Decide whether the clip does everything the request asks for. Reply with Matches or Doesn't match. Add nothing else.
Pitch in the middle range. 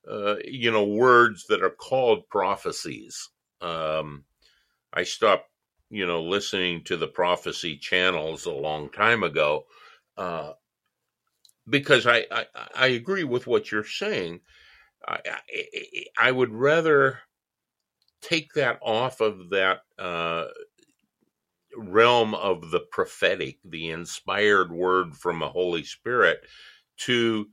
Doesn't match